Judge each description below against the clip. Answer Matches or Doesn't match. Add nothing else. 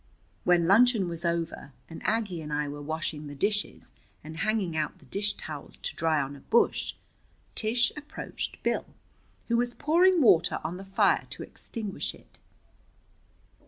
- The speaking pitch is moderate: Matches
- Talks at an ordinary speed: Matches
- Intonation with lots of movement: Matches